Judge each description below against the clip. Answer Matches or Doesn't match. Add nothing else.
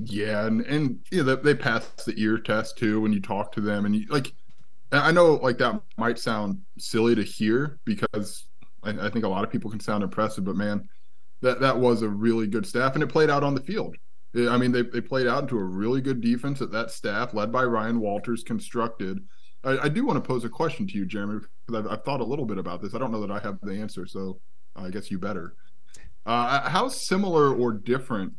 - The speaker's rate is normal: Doesn't match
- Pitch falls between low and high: Doesn't match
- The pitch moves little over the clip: Doesn't match